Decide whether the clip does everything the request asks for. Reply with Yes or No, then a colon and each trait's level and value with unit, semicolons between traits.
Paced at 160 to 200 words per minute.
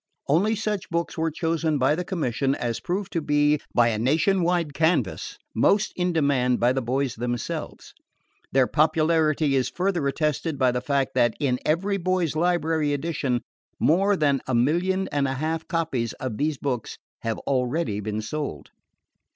Yes: average, 165 wpm